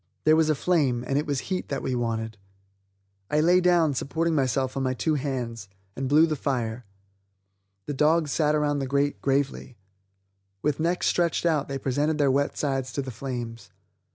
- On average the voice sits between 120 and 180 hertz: Yes, medium, 140 Hz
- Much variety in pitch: No, average, 3.1 semitones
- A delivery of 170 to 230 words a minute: Yes, average, 180 wpm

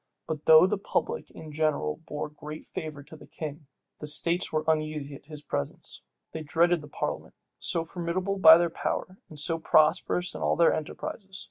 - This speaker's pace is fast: No, average, 185 wpm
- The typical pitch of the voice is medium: Yes, medium, 160 Hz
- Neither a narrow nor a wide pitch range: No, narrow, 2.3 semitones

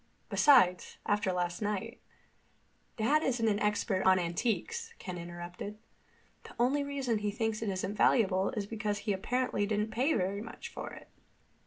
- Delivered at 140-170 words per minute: Yes, average, 155 wpm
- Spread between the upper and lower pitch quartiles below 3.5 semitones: No, average, 3.8 semitones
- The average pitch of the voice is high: Yes, high, 210 Hz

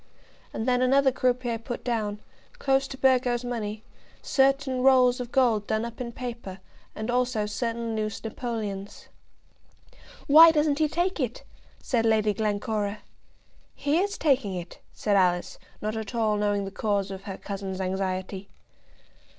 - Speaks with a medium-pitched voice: No, high, 230 Hz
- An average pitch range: Yes, average, 3.7 semitones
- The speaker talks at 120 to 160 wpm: Yes, average, 145 wpm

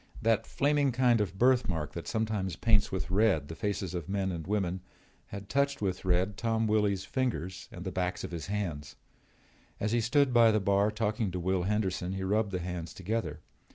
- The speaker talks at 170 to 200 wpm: Yes, average, 190 wpm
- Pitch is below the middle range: Yes, low, 100 Hz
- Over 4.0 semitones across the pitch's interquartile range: No, average, 3.4 semitones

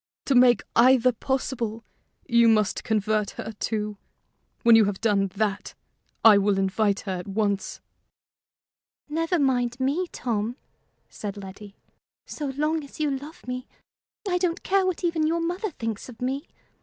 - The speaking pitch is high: Yes, high, 240 Hz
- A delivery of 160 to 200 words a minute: No, average, 150 wpm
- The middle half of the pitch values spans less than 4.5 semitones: No, wide, 5.6 semitones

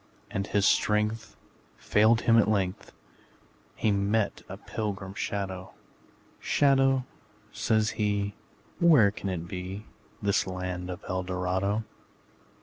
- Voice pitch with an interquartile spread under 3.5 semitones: Yes, narrow, 2.6 semitones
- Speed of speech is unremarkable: No, slow, 115 wpm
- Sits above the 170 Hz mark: No, low, 100 Hz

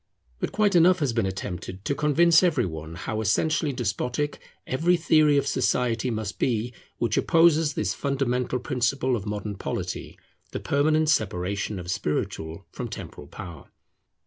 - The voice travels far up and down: Yes, wide, 6.7 semitones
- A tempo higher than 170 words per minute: No, average, 145 wpm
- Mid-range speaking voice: No, low, 125 Hz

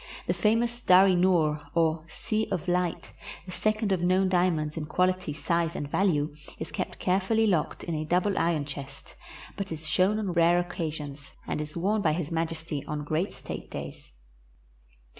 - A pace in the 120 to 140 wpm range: No, average, 180 wpm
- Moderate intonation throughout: Yes, average, 3.3 semitones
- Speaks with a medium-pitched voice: Yes, medium, 170 Hz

